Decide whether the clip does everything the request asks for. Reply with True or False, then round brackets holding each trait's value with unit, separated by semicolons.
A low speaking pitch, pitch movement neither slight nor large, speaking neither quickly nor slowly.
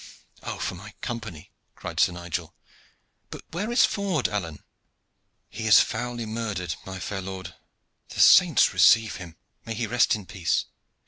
True (105 Hz; 4.4 semitones; 150 wpm)